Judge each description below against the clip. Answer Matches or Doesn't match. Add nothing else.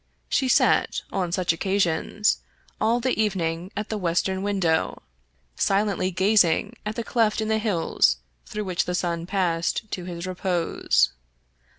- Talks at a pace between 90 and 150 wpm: Matches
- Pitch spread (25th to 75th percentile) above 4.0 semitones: Doesn't match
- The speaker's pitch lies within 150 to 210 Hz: Matches